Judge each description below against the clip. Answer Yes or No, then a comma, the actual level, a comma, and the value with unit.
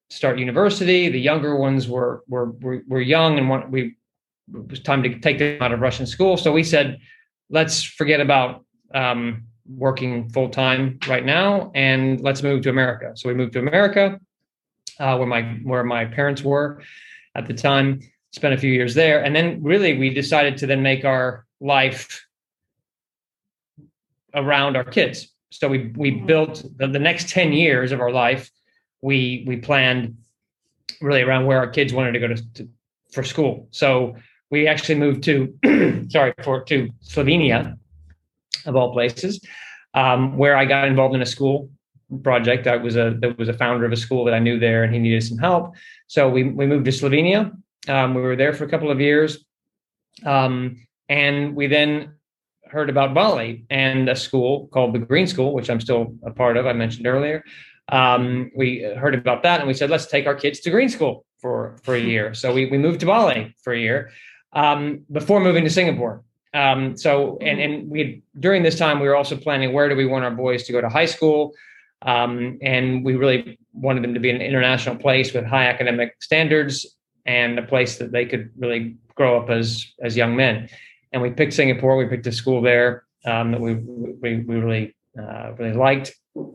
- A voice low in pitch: Yes, low, 130 Hz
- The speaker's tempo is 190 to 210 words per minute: Yes, average, 195 wpm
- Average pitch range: Yes, average, 3.0 semitones